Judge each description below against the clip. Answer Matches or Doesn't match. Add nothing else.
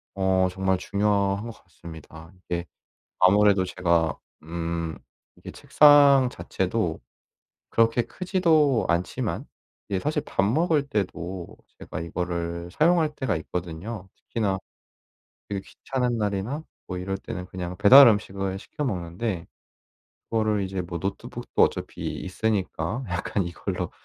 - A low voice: Matches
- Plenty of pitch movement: Doesn't match